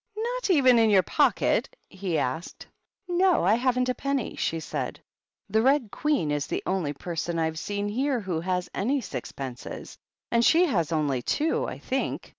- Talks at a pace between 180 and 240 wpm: No, average, 170 wpm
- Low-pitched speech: No, high, 205 Hz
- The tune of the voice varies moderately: No, wide, 8.7 semitones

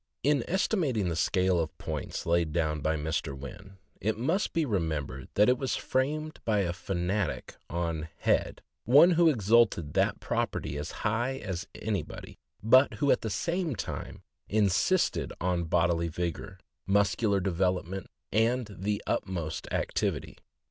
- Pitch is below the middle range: Yes, low, 100 Hz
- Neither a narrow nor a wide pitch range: No, wide, 6.3 semitones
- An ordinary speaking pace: Yes, average, 145 wpm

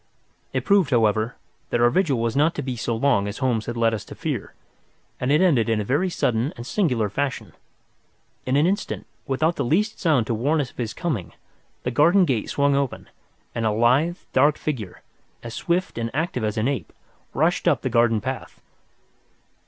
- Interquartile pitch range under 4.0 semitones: No, average, 5.0 semitones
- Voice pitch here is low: Yes, low, 130 Hz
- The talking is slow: No, average, 195 wpm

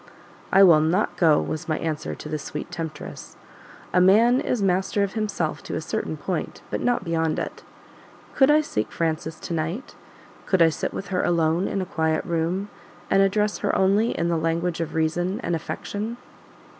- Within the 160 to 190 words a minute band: Yes, average, 185 wpm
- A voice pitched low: No, medium, 175 Hz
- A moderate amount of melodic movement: Yes, average, 3.6 semitones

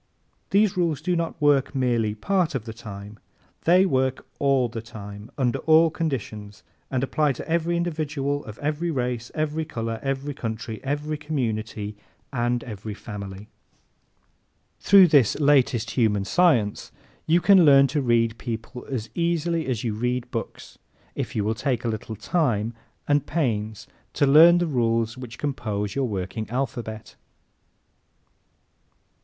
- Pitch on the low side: Yes, low, 125 Hz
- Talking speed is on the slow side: No, average, 145 wpm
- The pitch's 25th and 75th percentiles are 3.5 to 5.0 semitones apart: No, wide, 5.4 semitones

